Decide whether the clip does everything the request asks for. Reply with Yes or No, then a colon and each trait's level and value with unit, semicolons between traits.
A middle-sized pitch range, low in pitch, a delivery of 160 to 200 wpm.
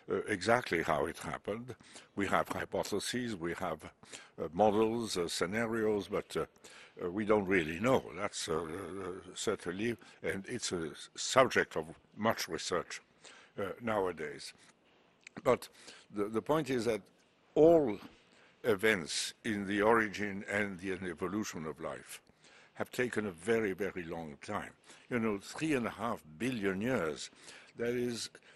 No: average, 3.3 semitones; low, 105 Hz; slow, 145 wpm